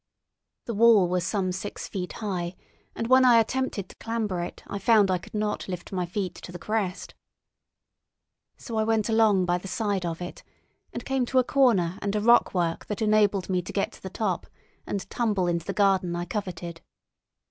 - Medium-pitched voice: No, high, 200 Hz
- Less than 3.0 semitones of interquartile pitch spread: No, average, 3.6 semitones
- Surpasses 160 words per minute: Yes, average, 195 wpm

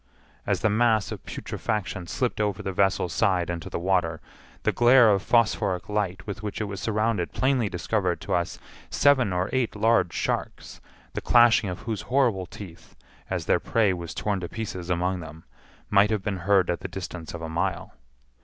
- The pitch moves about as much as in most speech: Yes, average, 3.5 semitones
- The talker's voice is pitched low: Yes, low, 100 Hz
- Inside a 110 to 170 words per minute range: No, average, 185 wpm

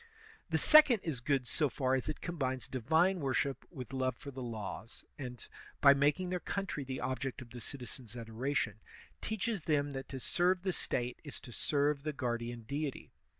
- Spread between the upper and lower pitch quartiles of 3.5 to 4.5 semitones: Yes, average, 3.8 semitones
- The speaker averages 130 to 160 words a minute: No, average, 190 wpm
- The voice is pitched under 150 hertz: Yes, low, 135 Hz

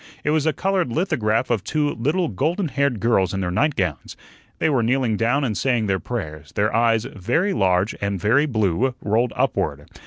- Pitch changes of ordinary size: No, wide, 6.1 semitones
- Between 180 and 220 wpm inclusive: Yes, average, 185 wpm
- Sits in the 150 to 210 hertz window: No, low, 115 Hz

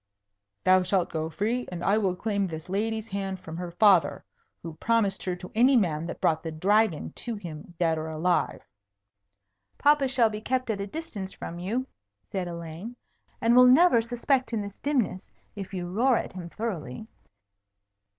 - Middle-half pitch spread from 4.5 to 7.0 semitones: Yes, average, 4.9 semitones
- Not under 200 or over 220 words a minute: No, average, 175 wpm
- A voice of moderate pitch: No, high, 195 Hz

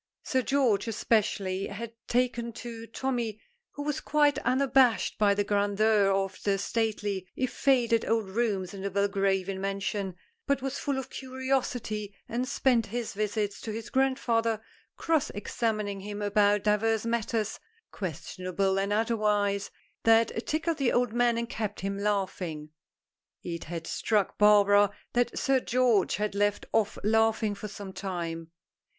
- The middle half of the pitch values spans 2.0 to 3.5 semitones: Yes, average, 3.1 semitones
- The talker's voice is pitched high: Yes, high, 215 Hz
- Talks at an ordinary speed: Yes, average, 145 wpm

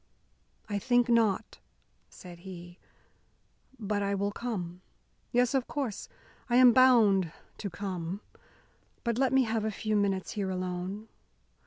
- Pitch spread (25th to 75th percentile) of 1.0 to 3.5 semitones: No, average, 4.1 semitones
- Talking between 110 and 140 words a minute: Yes, slow, 135 wpm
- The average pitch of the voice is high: Yes, high, 205 Hz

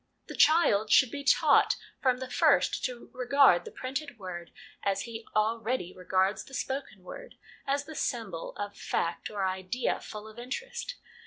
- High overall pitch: Yes, high, 235 Hz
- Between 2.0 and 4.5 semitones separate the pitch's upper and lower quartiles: No, wide, 5.5 semitones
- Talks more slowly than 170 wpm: Yes, average, 160 wpm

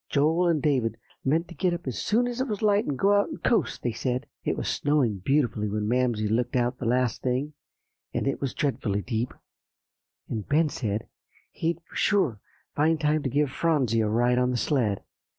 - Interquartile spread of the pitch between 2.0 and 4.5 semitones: No, wide, 5.4 semitones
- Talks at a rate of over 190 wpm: Yes, fast, 205 wpm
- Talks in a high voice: No, low, 135 Hz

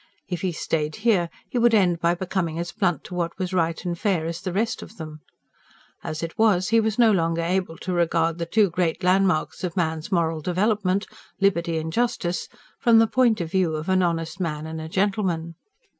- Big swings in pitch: No, average, 3.0 semitones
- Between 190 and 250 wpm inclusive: Yes, fast, 205 wpm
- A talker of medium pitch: Yes, medium, 175 Hz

